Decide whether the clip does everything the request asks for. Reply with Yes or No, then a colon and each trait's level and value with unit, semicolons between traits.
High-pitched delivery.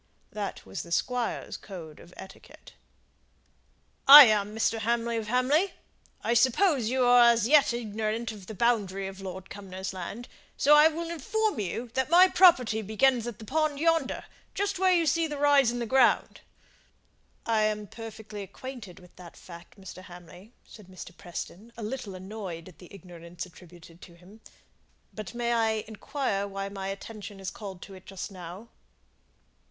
Yes: high, 220 Hz